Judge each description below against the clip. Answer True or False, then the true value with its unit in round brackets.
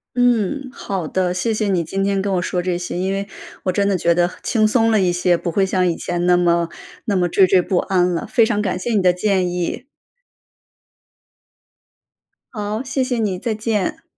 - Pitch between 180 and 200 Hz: True (190 Hz)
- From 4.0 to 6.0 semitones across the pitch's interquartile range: False (3.3 semitones)